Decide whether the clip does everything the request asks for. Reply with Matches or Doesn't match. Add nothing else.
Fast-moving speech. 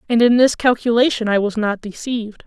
Doesn't match